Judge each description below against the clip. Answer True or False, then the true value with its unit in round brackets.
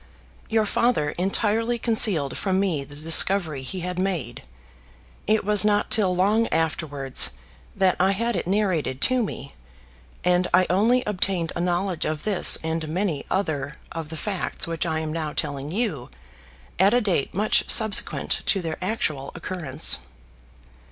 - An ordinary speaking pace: True (150 wpm)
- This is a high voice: False (180 Hz)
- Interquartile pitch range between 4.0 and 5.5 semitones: True (4.7 semitones)